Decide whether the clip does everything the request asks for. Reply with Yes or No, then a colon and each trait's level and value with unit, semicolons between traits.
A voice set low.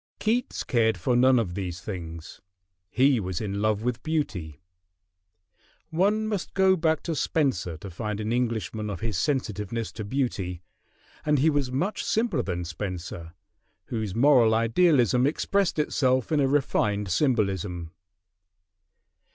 Yes: low, 115 Hz